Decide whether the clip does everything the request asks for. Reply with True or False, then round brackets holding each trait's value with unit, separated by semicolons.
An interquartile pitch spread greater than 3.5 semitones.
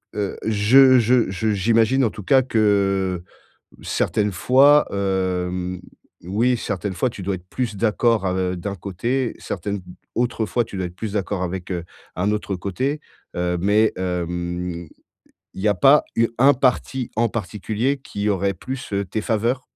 True (4.2 semitones)